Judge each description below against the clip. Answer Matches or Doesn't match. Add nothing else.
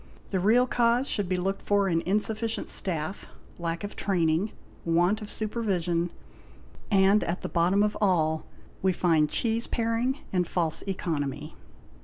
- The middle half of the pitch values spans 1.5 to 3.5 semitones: Doesn't match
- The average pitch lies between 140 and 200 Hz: Matches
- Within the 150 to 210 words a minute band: Doesn't match